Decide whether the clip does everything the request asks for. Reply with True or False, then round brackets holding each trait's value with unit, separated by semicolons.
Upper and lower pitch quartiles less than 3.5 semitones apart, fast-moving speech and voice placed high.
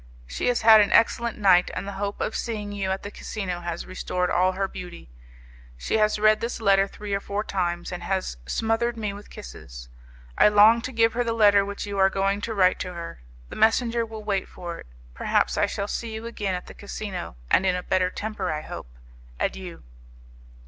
True (3.0 semitones; 210 wpm; 200 Hz)